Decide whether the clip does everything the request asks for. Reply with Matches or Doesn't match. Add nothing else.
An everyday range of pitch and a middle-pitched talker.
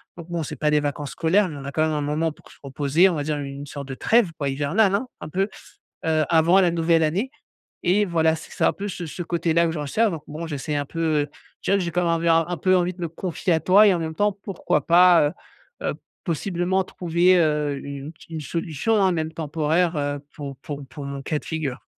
Matches